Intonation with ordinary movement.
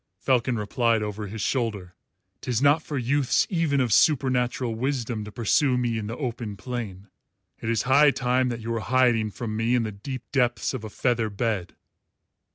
Yes: average, 3.0 semitones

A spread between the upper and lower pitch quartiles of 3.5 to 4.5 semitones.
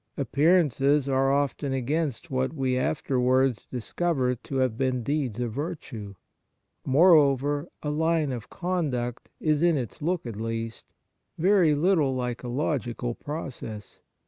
Yes: average, 3.8 semitones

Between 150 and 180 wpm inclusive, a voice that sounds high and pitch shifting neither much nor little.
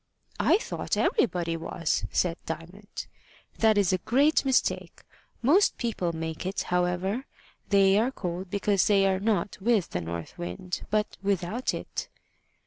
No: average, 140 wpm; high, 195 Hz; average, 3.8 semitones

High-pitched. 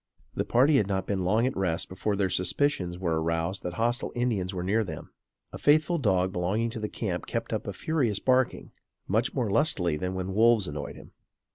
No: low, 100 Hz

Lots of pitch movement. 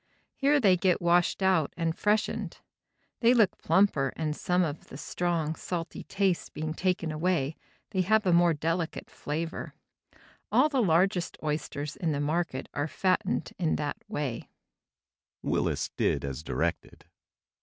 No: average, 3.3 semitones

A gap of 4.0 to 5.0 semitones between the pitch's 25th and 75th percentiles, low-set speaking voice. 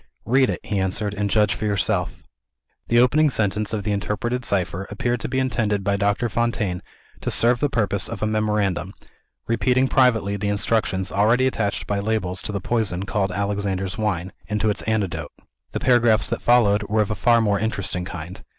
No: average, 2.8 semitones; low, 105 Hz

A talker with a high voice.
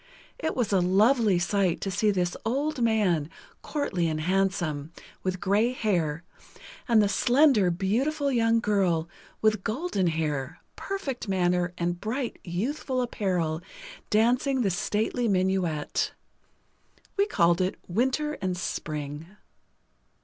Yes: high, 195 Hz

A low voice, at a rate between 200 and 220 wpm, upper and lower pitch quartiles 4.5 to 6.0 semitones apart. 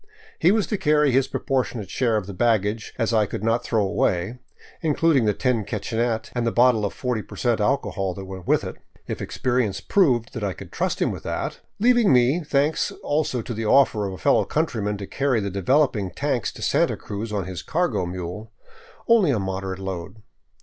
Yes: low, 115 Hz; fast, 205 wpm; average, 5.2 semitones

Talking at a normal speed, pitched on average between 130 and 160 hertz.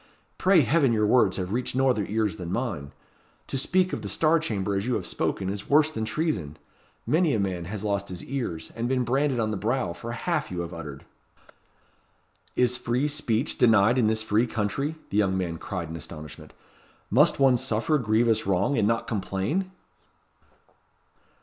No: average, 180 wpm; low, 110 Hz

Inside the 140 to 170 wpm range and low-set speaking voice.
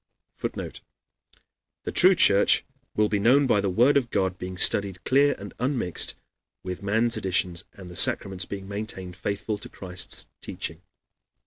Yes: average, 150 wpm; low, 100 Hz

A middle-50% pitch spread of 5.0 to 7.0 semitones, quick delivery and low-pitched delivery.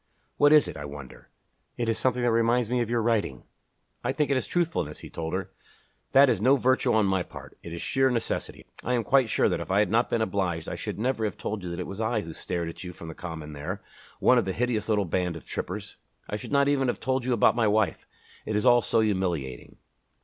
Yes: wide, 5.4 semitones; fast, 255 wpm; low, 110 Hz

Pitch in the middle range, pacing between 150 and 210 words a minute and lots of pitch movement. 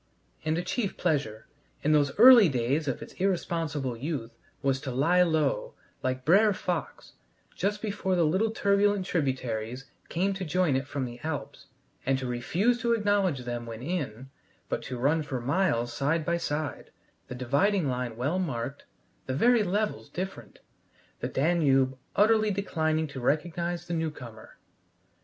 Yes: medium, 155 Hz; average, 155 wpm; wide, 6.2 semitones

